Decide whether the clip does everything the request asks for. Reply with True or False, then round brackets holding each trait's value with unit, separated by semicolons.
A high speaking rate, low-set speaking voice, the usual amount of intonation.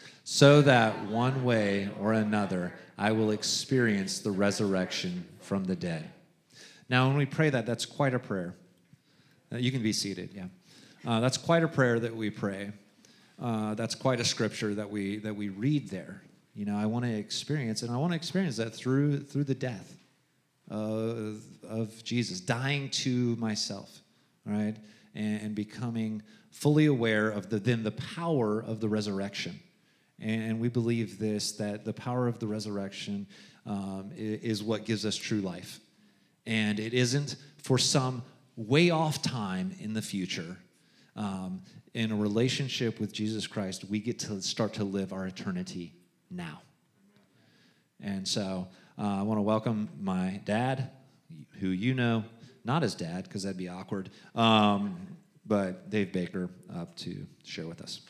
False (160 wpm; 110 Hz; 4.0 semitones)